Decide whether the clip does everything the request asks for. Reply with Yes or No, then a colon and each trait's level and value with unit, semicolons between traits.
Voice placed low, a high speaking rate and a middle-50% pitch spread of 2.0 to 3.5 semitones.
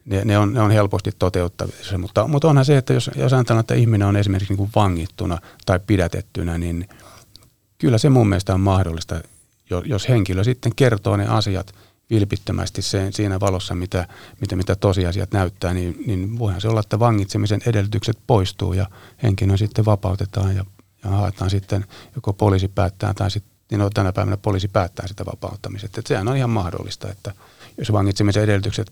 Yes: low, 100 Hz; fast, 180 wpm; narrow, 2.4 semitones